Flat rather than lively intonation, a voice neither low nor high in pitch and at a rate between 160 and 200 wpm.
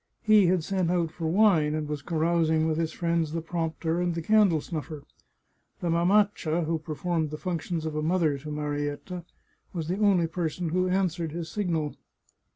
Yes: narrow, 2.3 semitones; medium, 165 Hz; average, 175 wpm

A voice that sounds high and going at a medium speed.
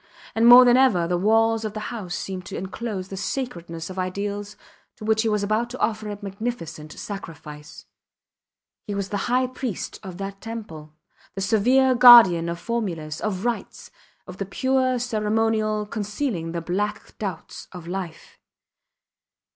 Yes: high, 205 Hz; average, 155 wpm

